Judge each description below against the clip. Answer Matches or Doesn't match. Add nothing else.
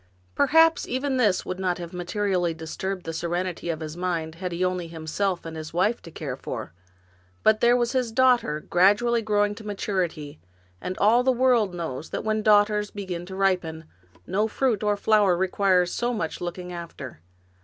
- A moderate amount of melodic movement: Matches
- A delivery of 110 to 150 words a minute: Doesn't match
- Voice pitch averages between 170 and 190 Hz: Matches